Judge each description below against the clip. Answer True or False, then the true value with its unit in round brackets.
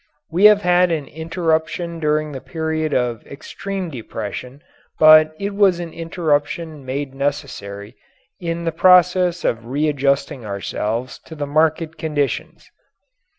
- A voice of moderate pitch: True (155 Hz)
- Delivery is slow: True (125 wpm)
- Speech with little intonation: False (3.5 semitones)